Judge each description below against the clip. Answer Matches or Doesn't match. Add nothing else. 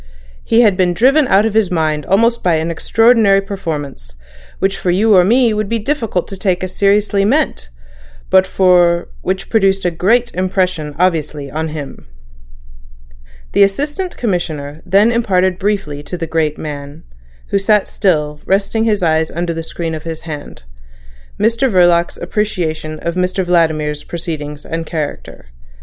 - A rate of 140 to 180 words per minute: Matches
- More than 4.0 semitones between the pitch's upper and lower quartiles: Matches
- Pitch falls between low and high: Matches